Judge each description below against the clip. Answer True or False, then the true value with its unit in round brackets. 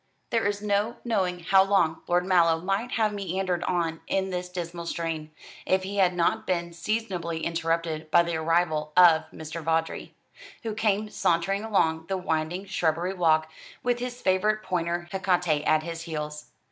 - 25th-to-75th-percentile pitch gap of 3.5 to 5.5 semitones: False (3.0 semitones)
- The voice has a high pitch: False (175 Hz)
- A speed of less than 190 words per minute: True (160 wpm)